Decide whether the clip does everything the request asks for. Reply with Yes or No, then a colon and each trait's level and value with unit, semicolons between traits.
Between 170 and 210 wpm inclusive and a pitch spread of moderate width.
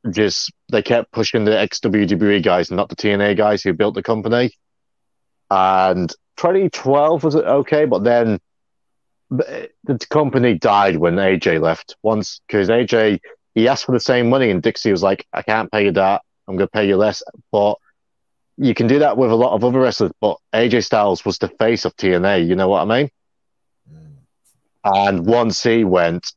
Yes: average, 180 wpm; average, 4.5 semitones